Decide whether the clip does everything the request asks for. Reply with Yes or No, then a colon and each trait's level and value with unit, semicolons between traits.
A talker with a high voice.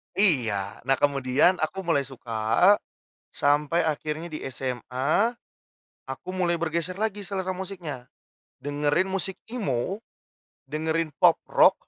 No: medium, 155 Hz